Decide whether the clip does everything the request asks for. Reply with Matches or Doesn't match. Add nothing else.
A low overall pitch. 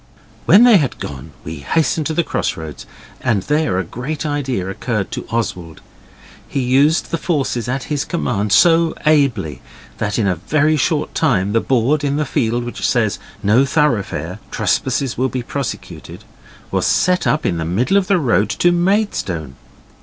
Matches